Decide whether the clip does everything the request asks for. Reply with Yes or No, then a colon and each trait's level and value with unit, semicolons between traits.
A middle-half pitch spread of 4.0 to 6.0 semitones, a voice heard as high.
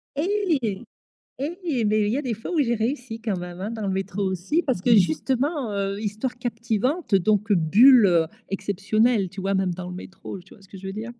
Yes: average, 4.3 semitones; high, 215 Hz